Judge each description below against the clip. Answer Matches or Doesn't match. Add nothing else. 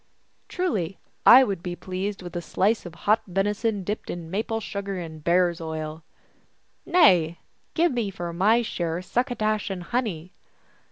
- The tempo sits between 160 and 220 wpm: Matches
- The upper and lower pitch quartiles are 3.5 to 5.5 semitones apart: Matches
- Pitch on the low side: Doesn't match